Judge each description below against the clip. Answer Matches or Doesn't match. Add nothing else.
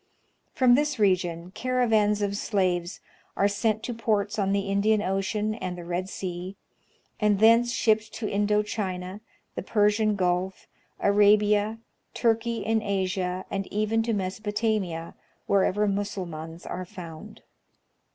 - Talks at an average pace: Doesn't match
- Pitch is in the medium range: Doesn't match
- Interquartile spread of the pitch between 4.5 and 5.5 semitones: Doesn't match